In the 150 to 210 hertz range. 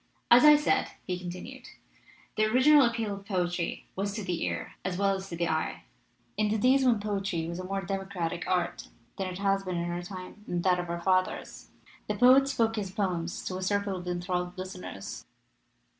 Yes: high, 190 Hz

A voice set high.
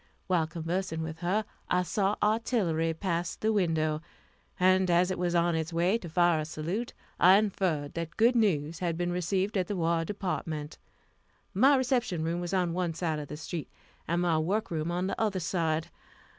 No: medium, 175 Hz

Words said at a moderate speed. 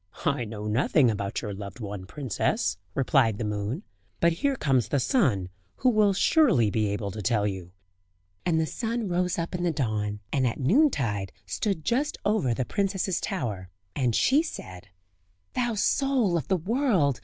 Yes: average, 170 wpm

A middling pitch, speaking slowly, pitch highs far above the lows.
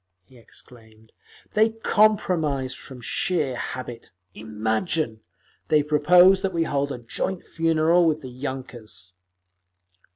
Yes: medium, 145 Hz; slow, 110 wpm; wide, 6.1 semitones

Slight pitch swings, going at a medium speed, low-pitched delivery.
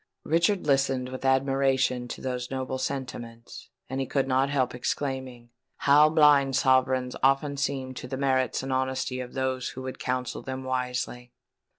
Yes: narrow, 1.2 semitones; average, 160 wpm; low, 130 Hz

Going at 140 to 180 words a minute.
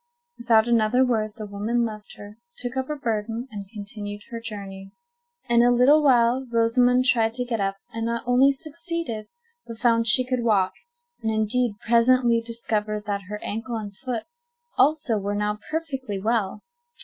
Yes: average, 165 wpm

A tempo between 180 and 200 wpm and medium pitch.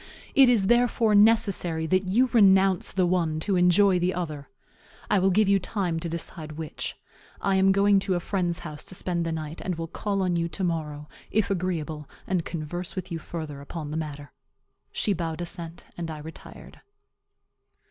Yes: average, 185 wpm; medium, 175 Hz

